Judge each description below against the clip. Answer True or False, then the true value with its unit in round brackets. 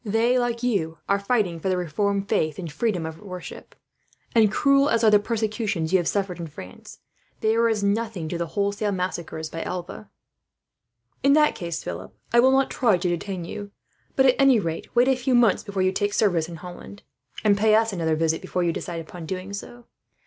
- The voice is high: True (200 Hz)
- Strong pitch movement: False (4.7 semitones)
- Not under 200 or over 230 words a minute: True (205 wpm)